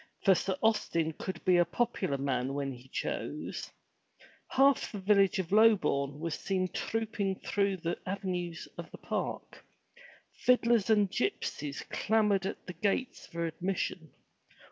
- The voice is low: No, high, 190 Hz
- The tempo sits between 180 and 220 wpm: No, average, 140 wpm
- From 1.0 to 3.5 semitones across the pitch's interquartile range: No, average, 4.0 semitones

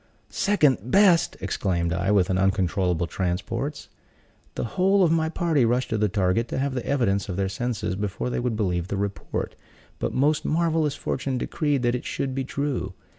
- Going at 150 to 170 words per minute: No, average, 180 wpm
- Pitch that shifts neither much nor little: No, wide, 6.8 semitones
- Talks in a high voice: No, low, 120 Hz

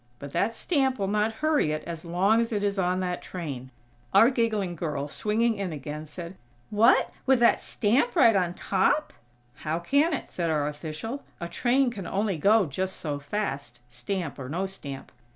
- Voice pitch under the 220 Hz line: Yes, high, 190 Hz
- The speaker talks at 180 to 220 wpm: Yes, average, 185 wpm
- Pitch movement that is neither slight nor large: No, wide, 6.6 semitones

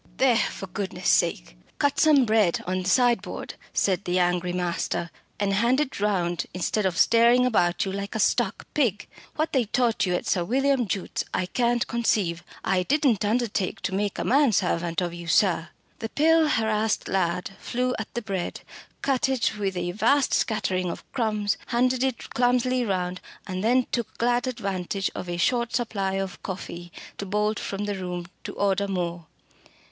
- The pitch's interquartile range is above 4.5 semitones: Yes, average, 4.9 semitones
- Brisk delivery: No, average, 175 wpm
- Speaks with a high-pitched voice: Yes, high, 205 Hz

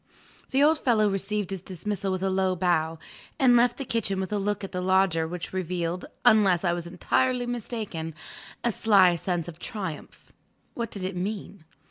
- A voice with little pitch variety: No, average, 3.3 semitones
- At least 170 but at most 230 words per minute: Yes, average, 180 wpm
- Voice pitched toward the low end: No, high, 190 Hz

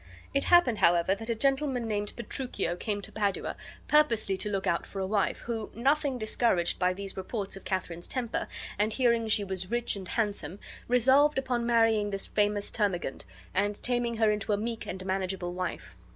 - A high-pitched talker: Yes, high, 210 Hz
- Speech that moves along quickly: No, average, 180 wpm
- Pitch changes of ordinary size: Yes, average, 3.7 semitones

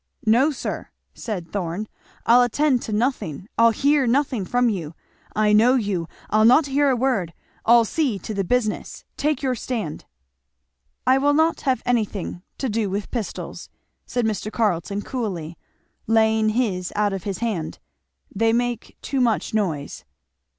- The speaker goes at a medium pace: Yes, average, 155 wpm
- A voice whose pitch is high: Yes, high, 225 Hz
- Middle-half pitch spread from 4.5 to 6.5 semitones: No, average, 3.8 semitones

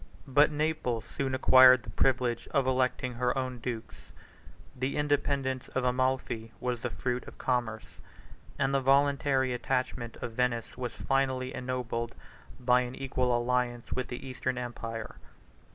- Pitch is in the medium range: No, low, 125 Hz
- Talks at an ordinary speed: Yes, average, 145 wpm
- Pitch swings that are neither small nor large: No, narrow, 1.4 semitones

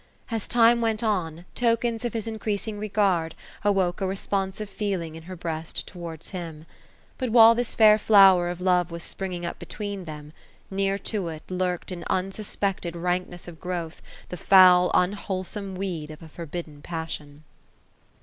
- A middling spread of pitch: Yes, average, 3.4 semitones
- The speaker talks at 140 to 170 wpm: Yes, average, 160 wpm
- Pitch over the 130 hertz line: Yes, medium, 185 Hz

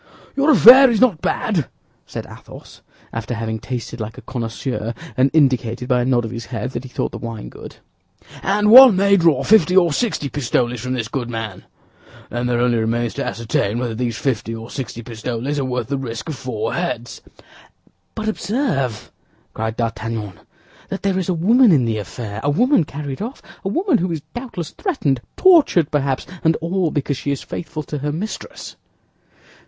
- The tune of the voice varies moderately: No, wide, 7.6 semitones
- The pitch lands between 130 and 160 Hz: Yes, low, 135 Hz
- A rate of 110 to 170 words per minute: No, average, 180 wpm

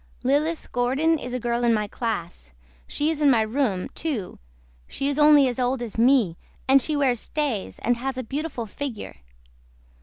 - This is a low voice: No, very high, 255 Hz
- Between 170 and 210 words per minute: Yes, average, 180 wpm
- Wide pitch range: No, average, 3.8 semitones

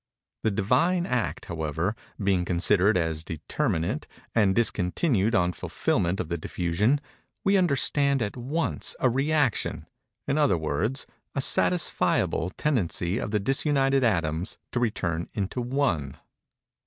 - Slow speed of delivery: Yes, slow, 120 wpm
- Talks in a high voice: No, low, 105 Hz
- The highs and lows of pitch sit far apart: Yes, wide, 7.6 semitones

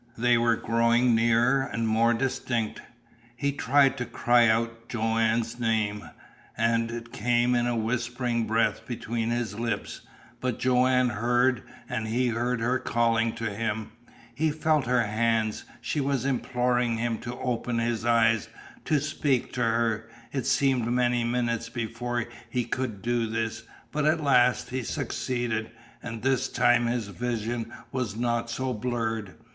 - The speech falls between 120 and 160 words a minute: Yes, average, 150 wpm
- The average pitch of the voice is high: No, low, 120 Hz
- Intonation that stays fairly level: Yes, narrow, 1.5 semitones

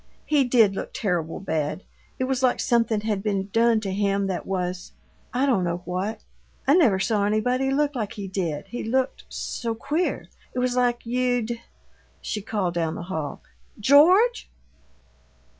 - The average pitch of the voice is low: No, high, 220 Hz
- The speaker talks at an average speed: Yes, average, 165 wpm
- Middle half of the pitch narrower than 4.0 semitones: No, average, 4.8 semitones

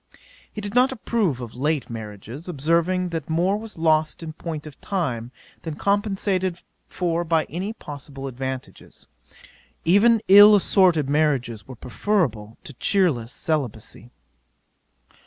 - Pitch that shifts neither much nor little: No, wide, 6.2 semitones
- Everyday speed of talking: No, slow, 125 wpm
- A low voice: No, medium, 160 Hz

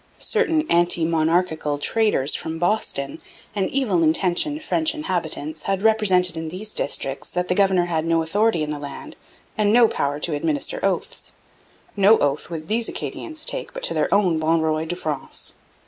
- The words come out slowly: No, average, 170 wpm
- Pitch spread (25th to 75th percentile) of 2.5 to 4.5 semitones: No, average, 5.1 semitones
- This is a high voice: No, medium, 175 Hz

